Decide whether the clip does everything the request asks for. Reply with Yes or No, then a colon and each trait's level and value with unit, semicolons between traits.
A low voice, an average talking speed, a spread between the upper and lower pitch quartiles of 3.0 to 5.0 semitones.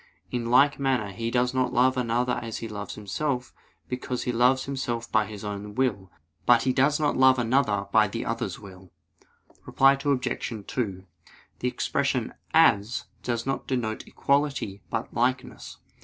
Yes: low, 120 Hz; average, 155 wpm; average, 3.5 semitones